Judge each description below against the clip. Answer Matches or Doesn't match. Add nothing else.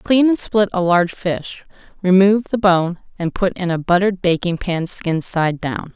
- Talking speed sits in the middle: Matches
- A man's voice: Doesn't match